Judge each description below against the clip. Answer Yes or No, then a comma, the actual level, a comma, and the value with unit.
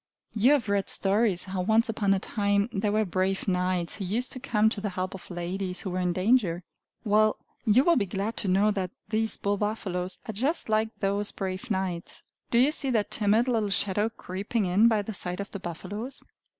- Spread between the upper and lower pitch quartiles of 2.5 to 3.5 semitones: Yes, average, 2.8 semitones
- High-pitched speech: Yes, high, 205 Hz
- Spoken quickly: Yes, fast, 210 wpm